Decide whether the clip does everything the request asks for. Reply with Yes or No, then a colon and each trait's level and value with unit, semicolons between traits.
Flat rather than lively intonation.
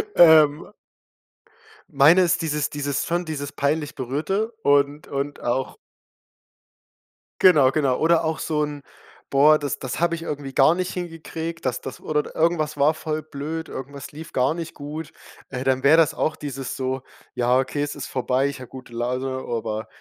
No: average, 3.1 semitones